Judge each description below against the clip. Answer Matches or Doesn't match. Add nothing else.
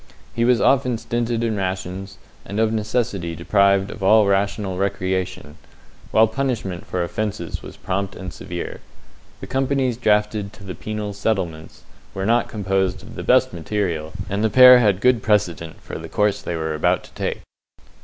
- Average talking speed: Matches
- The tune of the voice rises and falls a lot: Doesn't match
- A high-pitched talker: Doesn't match